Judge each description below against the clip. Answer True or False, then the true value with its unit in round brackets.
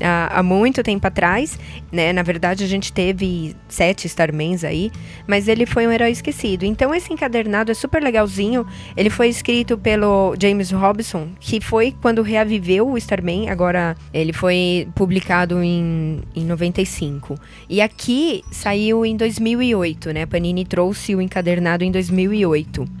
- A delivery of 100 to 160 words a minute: True (145 wpm)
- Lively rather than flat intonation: False (4.2 semitones)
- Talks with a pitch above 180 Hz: True (190 Hz)